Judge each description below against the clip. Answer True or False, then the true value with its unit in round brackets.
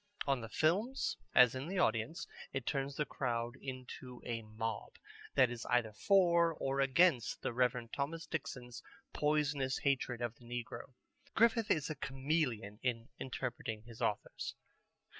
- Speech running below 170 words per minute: True (145 wpm)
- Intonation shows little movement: False (4.1 semitones)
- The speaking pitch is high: False (130 Hz)